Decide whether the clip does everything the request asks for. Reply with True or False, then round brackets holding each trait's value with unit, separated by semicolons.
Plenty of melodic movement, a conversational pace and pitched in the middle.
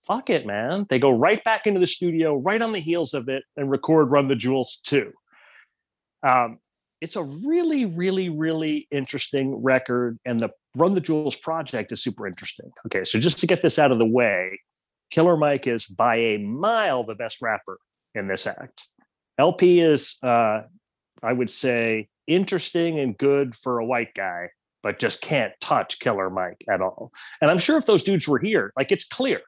True (6.0 semitones; 190 wpm; 145 Hz)